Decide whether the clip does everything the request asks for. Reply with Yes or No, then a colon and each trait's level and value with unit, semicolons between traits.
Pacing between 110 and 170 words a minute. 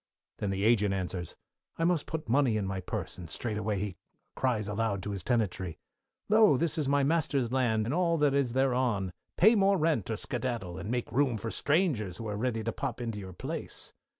No: fast, 205 wpm